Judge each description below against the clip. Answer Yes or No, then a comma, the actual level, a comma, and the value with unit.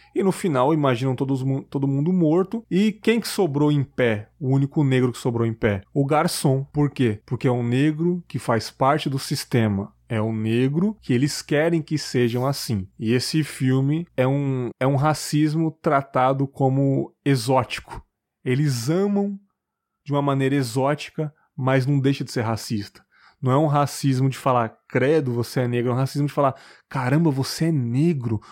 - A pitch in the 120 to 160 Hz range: Yes, medium, 140 Hz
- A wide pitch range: No, average, 3.3 semitones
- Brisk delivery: No, average, 175 wpm